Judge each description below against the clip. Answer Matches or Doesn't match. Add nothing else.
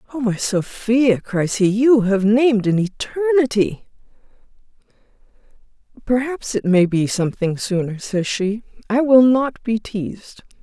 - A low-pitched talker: Doesn't match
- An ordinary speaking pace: Doesn't match